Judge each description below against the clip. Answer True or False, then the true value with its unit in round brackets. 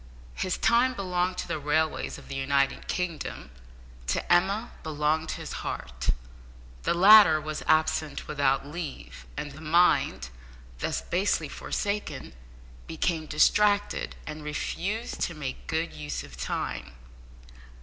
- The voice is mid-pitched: True (155 Hz)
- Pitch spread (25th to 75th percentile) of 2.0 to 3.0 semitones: False (4.1 semitones)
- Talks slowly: True (125 wpm)